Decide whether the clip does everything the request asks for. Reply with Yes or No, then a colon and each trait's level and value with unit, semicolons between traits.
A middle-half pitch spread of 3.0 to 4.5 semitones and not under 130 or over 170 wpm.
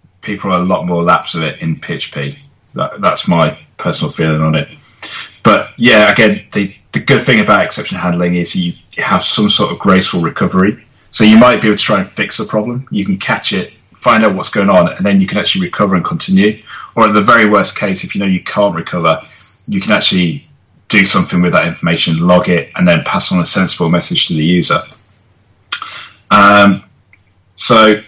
No: average, 3.5 semitones; fast, 205 wpm